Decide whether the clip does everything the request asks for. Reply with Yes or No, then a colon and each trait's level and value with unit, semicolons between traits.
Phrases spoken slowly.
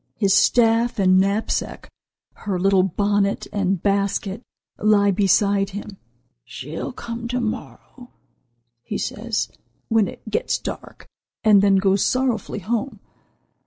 Yes: slow, 120 wpm